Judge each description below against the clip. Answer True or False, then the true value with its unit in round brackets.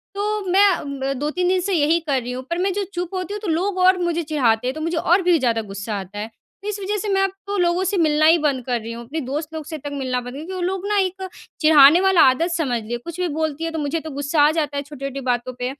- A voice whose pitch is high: True (315 Hz)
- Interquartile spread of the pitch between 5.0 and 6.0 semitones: True (5.3 semitones)